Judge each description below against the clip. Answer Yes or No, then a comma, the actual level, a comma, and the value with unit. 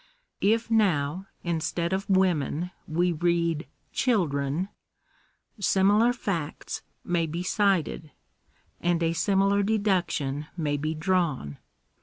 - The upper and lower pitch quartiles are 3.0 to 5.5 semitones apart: Yes, average, 3.9 semitones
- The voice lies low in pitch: No, medium, 175 Hz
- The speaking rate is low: Yes, slow, 100 wpm